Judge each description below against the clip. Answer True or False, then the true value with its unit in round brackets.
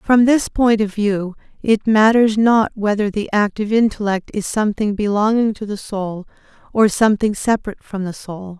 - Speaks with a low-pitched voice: False (210 Hz)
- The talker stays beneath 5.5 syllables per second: True (5.0 syllables/s)